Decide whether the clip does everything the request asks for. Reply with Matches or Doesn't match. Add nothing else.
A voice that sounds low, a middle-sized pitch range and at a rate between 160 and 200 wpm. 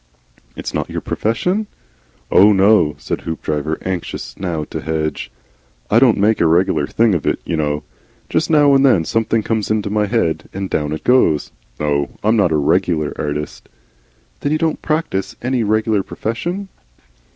Doesn't match